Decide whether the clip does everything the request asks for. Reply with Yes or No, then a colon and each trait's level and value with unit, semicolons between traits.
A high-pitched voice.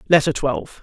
No: medium, 140 Hz